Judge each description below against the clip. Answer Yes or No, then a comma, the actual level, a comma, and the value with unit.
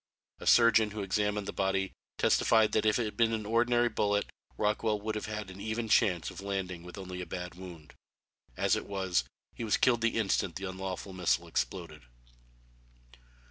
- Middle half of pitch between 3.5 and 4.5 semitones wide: No, average, 2.8 semitones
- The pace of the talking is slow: No, average, 180 wpm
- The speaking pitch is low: Yes, low, 105 Hz